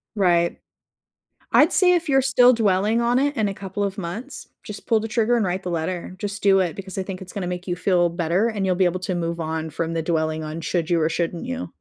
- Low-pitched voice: No, medium, 185 Hz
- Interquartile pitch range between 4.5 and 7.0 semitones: No, average, 4.1 semitones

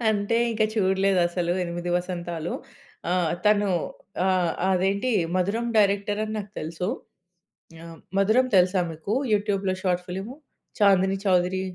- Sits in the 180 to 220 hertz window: Yes, high, 190 Hz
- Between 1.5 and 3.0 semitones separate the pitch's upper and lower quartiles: Yes, narrow, 2.4 semitones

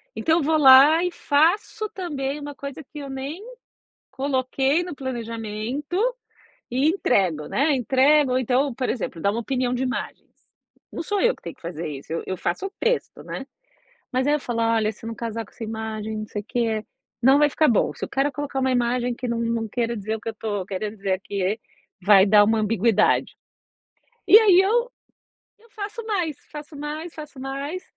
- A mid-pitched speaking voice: No, very high, 260 Hz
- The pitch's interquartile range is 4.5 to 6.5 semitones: Yes, average, 5.2 semitones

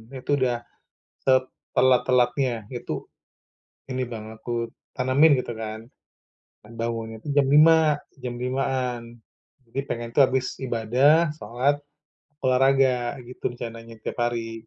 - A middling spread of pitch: No, narrow, 2.3 semitones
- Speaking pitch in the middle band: No, low, 125 Hz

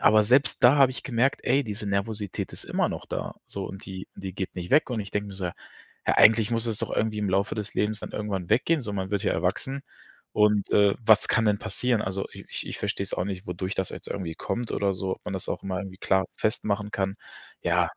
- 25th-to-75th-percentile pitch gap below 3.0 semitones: Yes, narrow, 2.5 semitones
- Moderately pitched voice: No, low, 105 Hz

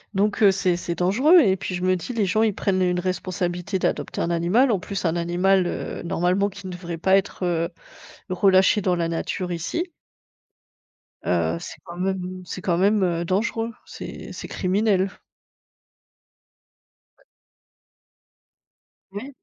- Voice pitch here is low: No, medium, 185 Hz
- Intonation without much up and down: Yes, narrow, 2.3 semitones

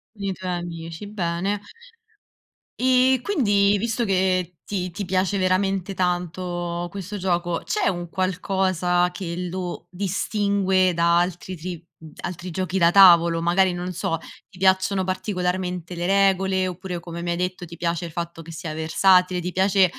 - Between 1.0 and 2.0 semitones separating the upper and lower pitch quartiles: Yes, narrow, 1.7 semitones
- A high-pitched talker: No, medium, 180 Hz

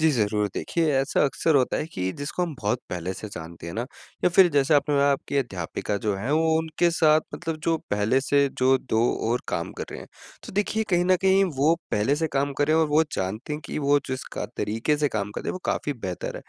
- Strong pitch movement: Yes, wide, 6.6 semitones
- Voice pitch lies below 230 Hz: Yes, medium, 140 Hz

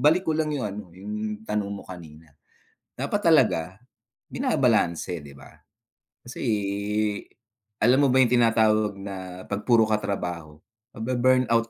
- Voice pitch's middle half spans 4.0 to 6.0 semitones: Yes, average, 4.8 semitones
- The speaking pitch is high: No, low, 105 Hz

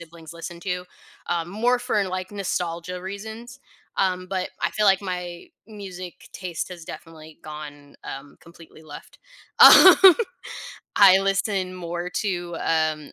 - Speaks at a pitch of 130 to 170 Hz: No, medium, 180 Hz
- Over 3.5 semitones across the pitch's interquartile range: No, average, 2.8 semitones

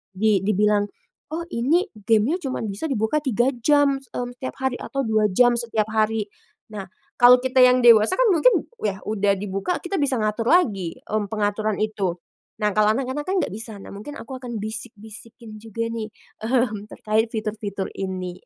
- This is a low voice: No, high, 220 Hz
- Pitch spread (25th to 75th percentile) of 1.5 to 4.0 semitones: Yes, average, 3.4 semitones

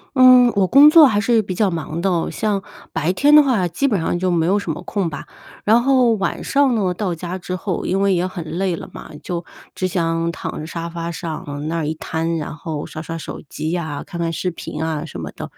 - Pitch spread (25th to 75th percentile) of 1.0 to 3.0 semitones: No, average, 3.9 semitones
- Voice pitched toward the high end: No, medium, 175 Hz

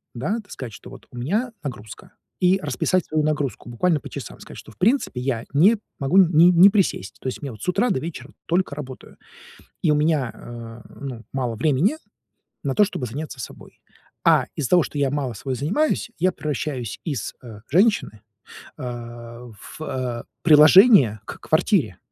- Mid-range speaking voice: Yes, medium, 145 Hz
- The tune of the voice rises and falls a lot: Yes, wide, 6.3 semitones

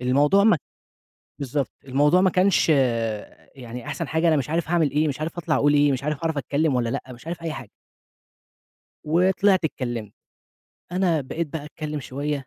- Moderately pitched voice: Yes, medium, 150 Hz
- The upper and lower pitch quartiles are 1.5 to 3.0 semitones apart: No, average, 3.7 semitones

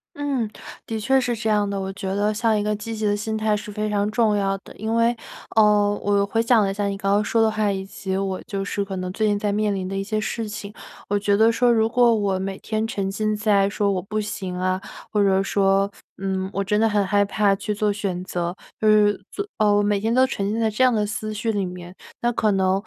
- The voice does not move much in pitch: Yes, narrow, 1.8 semitones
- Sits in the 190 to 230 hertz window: Yes, high, 205 Hz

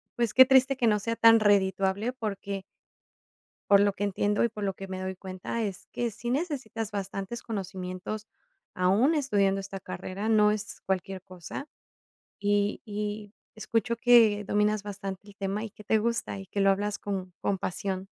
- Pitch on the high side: Yes, high, 205 Hz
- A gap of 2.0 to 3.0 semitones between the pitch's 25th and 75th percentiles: Yes, narrow, 2.4 semitones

